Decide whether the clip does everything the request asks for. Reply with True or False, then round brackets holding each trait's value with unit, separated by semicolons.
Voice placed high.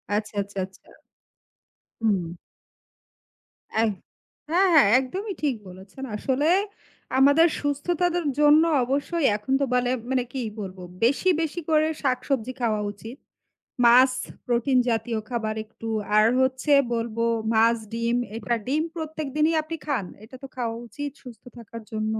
True (255 Hz)